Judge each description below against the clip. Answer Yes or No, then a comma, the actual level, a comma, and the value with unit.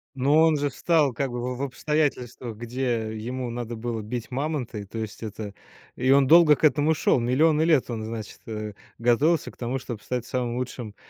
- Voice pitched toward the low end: Yes, low, 125 Hz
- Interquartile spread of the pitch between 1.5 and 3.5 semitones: No, average, 3.9 semitones